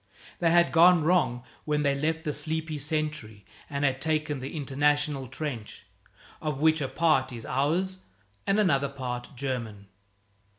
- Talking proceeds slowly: No, average, 145 wpm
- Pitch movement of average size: Yes, average, 3.2 semitones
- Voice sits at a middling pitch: Yes, medium, 150 Hz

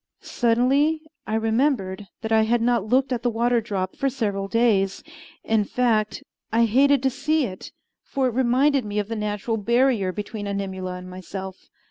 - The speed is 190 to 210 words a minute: No, average, 170 wpm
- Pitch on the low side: No, high, 225 Hz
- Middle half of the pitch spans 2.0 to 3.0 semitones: No, average, 3.7 semitones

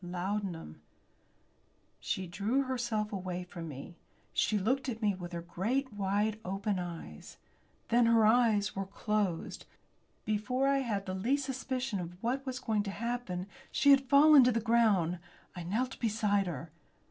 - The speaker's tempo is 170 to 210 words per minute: No, average, 155 wpm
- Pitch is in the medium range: No, high, 210 Hz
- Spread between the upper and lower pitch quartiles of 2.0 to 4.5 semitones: No, average, 4.9 semitones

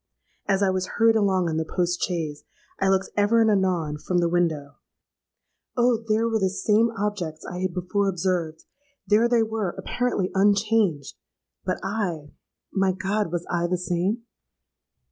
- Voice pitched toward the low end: No, high, 190 Hz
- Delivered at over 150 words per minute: No, average, 145 wpm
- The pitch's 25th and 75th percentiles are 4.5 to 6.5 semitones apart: No, average, 3.5 semitones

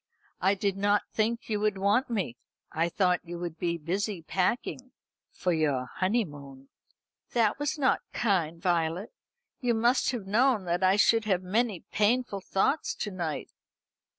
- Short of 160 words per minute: Yes, average, 150 wpm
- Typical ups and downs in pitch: Yes, average, 4.6 semitones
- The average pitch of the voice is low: No, high, 195 Hz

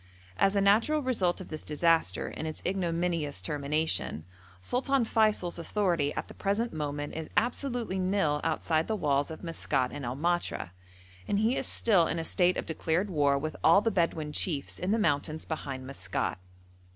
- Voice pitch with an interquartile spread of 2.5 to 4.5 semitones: No, average, 5.2 semitones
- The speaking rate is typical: Yes, average, 175 wpm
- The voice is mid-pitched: Yes, medium, 165 Hz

